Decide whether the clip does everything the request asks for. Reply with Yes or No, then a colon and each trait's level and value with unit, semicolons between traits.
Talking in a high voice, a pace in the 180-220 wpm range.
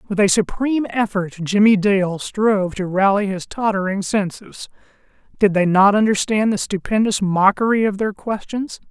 No: high, 200 Hz; average, 150 wpm